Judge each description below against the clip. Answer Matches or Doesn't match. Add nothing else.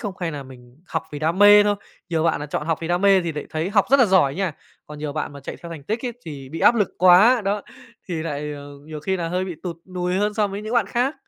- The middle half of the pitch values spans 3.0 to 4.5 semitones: Doesn't match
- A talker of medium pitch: Matches